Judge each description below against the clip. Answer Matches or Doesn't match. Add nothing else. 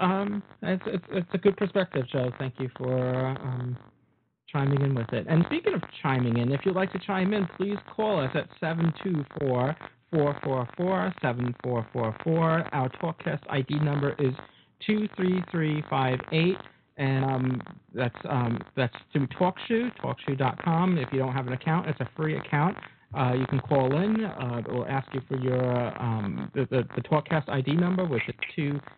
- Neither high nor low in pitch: Matches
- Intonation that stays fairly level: Doesn't match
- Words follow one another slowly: Doesn't match